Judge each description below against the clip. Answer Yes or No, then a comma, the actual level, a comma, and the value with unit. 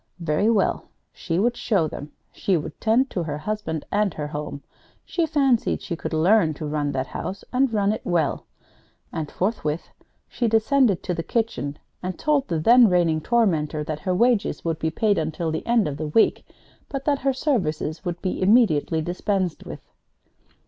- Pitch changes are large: Yes, wide, 6.4 semitones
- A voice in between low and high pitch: Yes, medium, 180 Hz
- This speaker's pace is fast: No, average, 180 wpm